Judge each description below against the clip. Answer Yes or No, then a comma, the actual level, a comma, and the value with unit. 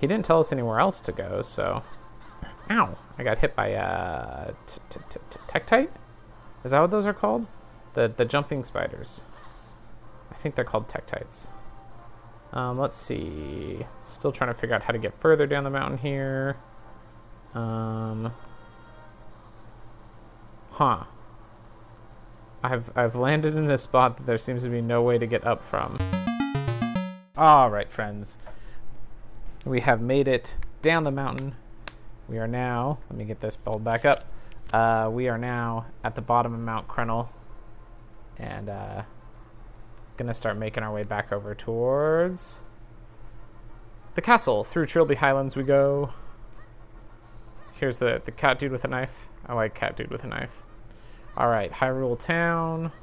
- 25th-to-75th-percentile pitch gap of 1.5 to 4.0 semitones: Yes, average, 3.1 semitones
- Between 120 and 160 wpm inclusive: Yes, average, 150 wpm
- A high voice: No, low, 115 Hz